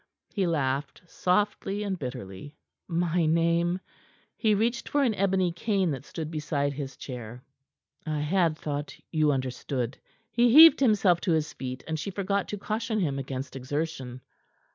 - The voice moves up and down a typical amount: No, wide, 6.1 semitones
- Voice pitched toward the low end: No, medium, 165 Hz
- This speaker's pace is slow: No, average, 150 wpm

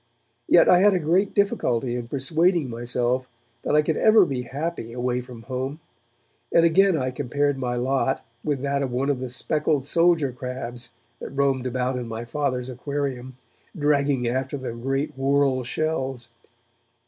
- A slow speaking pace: No, average, 160 wpm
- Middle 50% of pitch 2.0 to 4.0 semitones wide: Yes, average, 3.0 semitones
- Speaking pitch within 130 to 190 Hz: Yes, low, 135 Hz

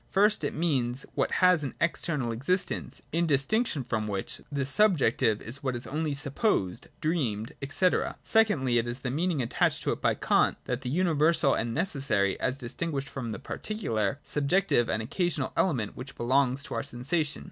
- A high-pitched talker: No, medium, 140 Hz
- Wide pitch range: Yes, wide, 5.7 semitones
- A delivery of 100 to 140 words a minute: No, average, 170 wpm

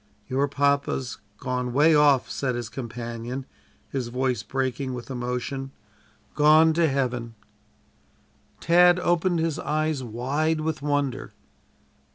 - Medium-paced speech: No, slow, 115 wpm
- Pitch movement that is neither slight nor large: Yes, average, 3.6 semitones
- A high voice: No, low, 135 Hz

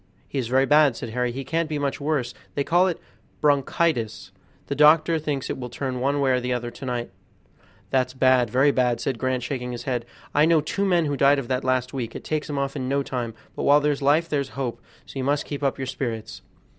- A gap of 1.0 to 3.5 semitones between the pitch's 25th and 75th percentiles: Yes, average, 2.7 semitones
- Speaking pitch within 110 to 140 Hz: Yes, low, 135 Hz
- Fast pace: Yes, fast, 235 wpm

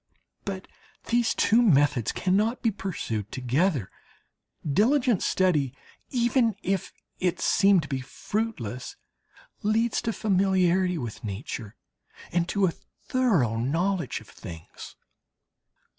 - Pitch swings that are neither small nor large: No, wide, 8.1 semitones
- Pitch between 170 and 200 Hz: Yes, medium, 185 Hz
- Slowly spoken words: Yes, slow, 110 wpm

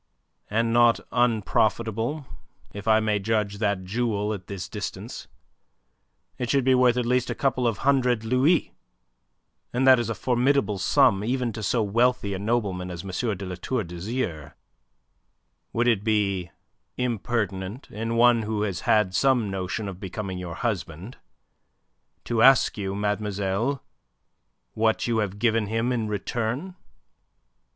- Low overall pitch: Yes, low, 110 Hz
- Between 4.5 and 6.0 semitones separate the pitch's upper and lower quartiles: No, average, 3.4 semitones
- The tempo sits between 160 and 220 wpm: No, average, 145 wpm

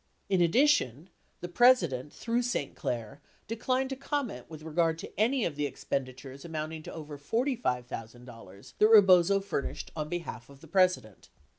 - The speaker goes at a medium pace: Yes, average, 155 wpm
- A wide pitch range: Yes, wide, 8.1 semitones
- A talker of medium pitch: Yes, medium, 165 Hz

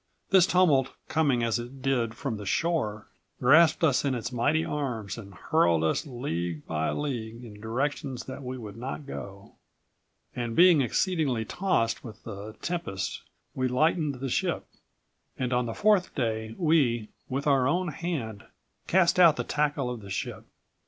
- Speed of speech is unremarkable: Yes, average, 160 wpm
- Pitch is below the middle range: Yes, low, 125 Hz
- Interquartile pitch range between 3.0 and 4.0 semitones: No, average, 5.1 semitones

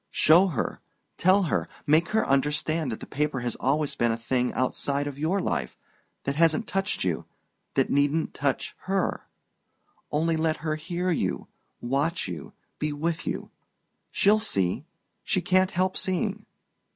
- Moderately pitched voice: Yes, medium, 155 Hz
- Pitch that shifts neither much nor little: Yes, average, 4.7 semitones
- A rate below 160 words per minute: Yes, average, 145 wpm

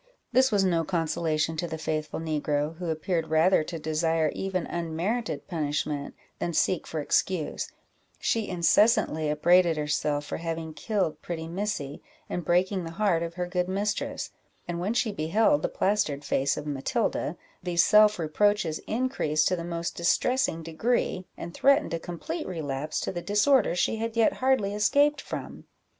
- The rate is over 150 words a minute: Yes, average, 160 wpm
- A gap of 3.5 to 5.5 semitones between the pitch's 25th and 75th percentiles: Yes, average, 4.5 semitones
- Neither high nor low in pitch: Yes, medium, 170 Hz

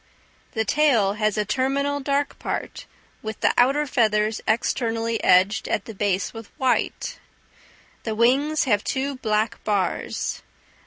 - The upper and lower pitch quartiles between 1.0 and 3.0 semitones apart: No, average, 4.2 semitones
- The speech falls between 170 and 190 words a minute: No, slow, 135 wpm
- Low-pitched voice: No, high, 225 Hz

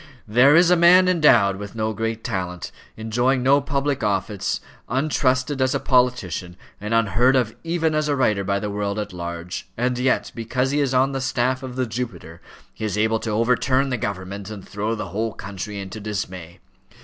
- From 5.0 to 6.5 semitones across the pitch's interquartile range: No, average, 4.5 semitones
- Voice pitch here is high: No, low, 115 Hz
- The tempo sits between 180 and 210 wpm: Yes, average, 190 wpm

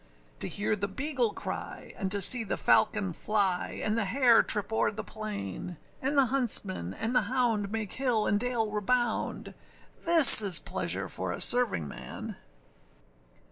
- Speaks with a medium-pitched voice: No, high, 220 Hz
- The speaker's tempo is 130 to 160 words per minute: Yes, average, 155 wpm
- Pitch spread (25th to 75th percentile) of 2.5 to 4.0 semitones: Yes, average, 3.6 semitones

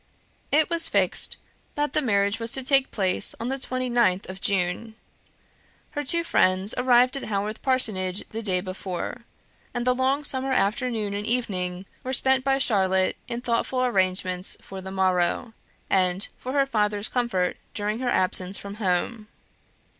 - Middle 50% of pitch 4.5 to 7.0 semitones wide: Yes, average, 5.2 semitones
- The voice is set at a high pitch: Yes, high, 220 Hz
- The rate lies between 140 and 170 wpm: Yes, average, 155 wpm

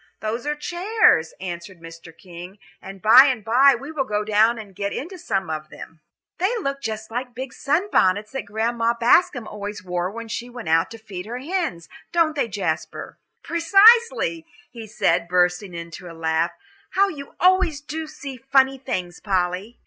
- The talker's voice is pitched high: Yes, high, 225 Hz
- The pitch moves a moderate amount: No, wide, 7.2 semitones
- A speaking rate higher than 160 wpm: Yes, average, 175 wpm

